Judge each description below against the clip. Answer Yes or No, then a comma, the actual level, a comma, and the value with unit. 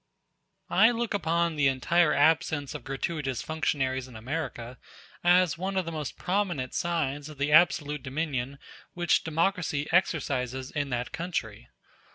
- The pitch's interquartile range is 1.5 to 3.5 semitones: No, average, 4.3 semitones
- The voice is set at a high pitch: No, medium, 150 Hz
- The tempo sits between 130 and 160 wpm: Yes, average, 140 wpm